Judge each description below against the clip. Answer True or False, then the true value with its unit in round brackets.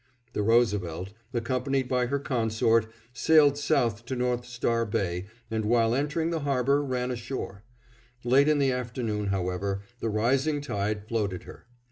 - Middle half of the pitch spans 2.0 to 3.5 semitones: False (4.2 semitones)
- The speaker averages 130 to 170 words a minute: True (145 wpm)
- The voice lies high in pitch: False (120 Hz)